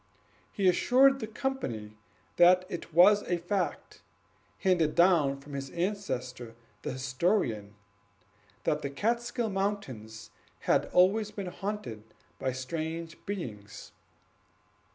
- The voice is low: No, medium, 170 Hz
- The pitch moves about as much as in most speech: No, wide, 7.7 semitones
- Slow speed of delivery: Yes, slow, 110 wpm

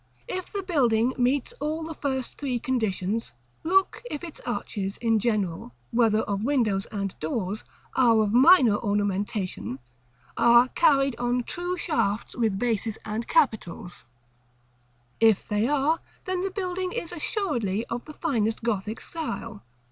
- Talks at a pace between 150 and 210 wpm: No, average, 140 wpm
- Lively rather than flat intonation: Yes, wide, 6.0 semitones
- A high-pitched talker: Yes, high, 235 Hz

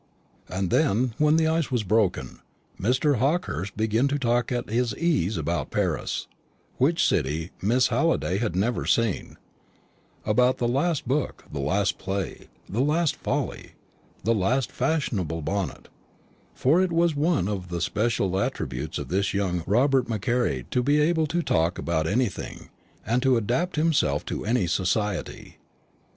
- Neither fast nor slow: Yes, average, 150 wpm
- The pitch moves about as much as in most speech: No, wide, 6.6 semitones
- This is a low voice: Yes, low, 115 Hz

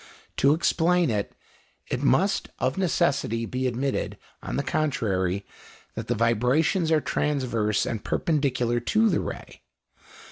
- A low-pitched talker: Yes, low, 130 Hz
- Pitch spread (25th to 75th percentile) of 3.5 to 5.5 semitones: Yes, average, 5.2 semitones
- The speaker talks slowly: Yes, slow, 130 wpm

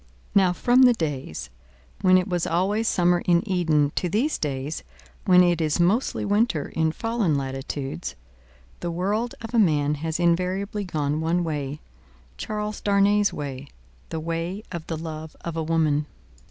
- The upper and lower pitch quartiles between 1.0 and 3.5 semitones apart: No, average, 4.4 semitones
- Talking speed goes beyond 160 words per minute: No, average, 155 wpm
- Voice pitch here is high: No, medium, 170 Hz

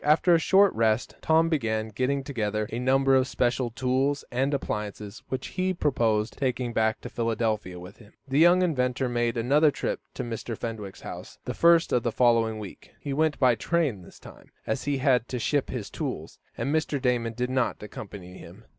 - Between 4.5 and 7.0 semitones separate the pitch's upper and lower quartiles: No, average, 4.1 semitones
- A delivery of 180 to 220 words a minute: Yes, average, 190 wpm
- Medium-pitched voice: No, low, 125 Hz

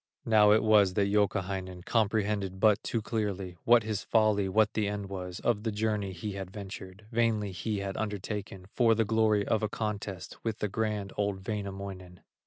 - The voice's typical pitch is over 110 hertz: No, low, 105 Hz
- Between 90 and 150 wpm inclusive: No, average, 180 wpm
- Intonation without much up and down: Yes, narrow, 2.0 semitones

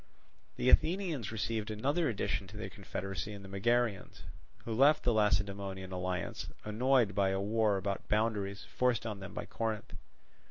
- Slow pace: No, average, 155 wpm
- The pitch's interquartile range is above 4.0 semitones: No, average, 3.0 semitones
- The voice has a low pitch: Yes, low, 105 Hz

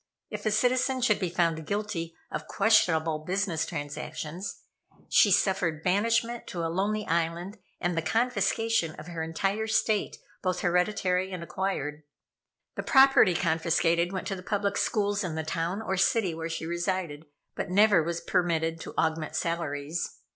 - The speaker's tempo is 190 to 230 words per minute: No, average, 155 wpm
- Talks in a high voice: No, medium, 180 Hz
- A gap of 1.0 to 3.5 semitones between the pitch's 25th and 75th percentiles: No, average, 3.9 semitones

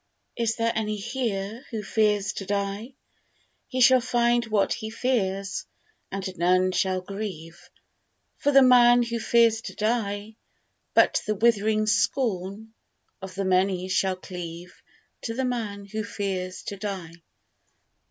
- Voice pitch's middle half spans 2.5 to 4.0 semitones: Yes, average, 3.4 semitones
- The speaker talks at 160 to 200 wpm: No, slow, 135 wpm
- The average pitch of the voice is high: Yes, high, 210 Hz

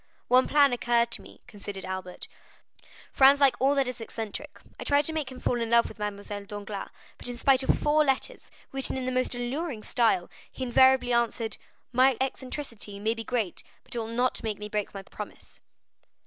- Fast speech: No, average, 195 wpm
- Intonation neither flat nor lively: Yes, average, 3.8 semitones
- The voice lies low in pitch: No, high, 240 Hz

